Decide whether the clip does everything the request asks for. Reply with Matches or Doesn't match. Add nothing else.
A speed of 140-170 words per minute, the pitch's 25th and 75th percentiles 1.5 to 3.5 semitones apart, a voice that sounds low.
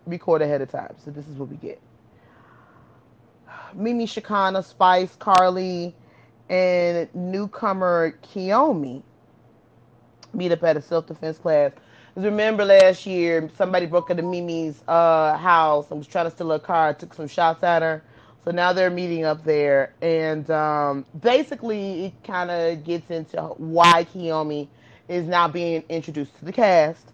Doesn't match